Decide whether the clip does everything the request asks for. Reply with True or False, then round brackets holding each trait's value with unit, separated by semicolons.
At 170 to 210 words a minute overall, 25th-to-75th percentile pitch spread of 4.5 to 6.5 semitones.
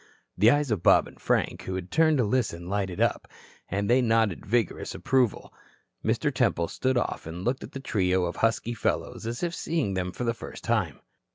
True (200 wpm; 5.1 semitones)